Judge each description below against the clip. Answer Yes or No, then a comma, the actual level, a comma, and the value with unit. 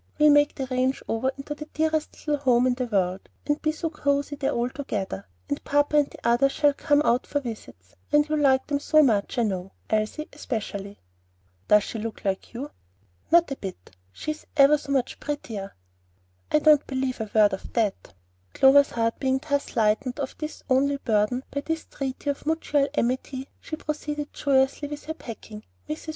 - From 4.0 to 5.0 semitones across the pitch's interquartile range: Yes, average, 4.4 semitones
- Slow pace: No, average, 190 wpm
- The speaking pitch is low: No, very high, 270 Hz